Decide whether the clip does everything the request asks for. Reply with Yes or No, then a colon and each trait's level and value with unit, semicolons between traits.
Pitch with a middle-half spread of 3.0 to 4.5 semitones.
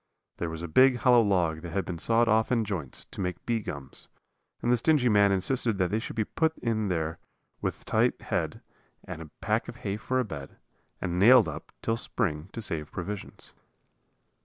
No: average, 5.2 semitones